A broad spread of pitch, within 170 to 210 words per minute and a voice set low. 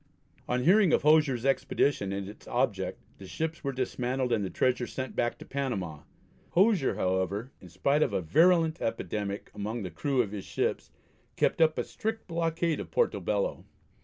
Yes: wide, 8.0 semitones; average, 175 wpm; low, 130 Hz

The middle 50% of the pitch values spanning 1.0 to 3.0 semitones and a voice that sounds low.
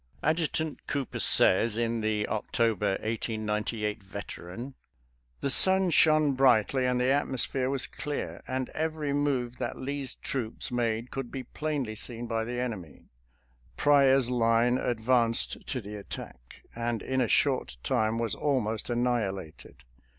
No: average, 3.6 semitones; low, 120 Hz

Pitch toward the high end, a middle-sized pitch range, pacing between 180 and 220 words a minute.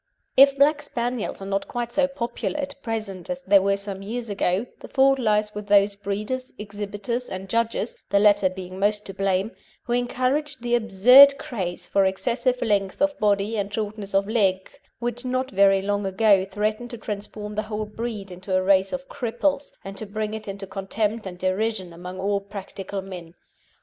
Yes: high, 210 Hz; average, 3.6 semitones; average, 185 wpm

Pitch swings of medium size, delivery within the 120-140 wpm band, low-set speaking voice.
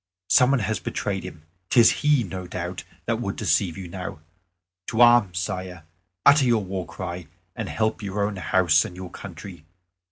No: average, 3.6 semitones; average, 180 wpm; very low, 95 Hz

